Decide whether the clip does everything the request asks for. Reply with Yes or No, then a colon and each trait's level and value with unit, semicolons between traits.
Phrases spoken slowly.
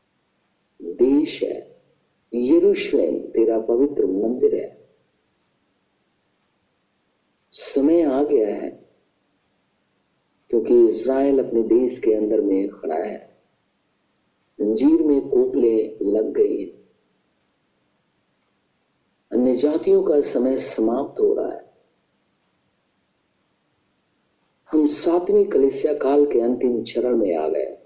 Yes: slow, 95 wpm